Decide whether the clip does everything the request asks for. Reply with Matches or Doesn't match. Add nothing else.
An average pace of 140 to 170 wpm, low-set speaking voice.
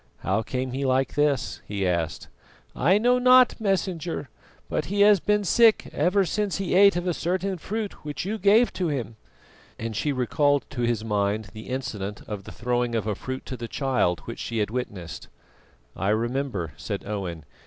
Doesn't match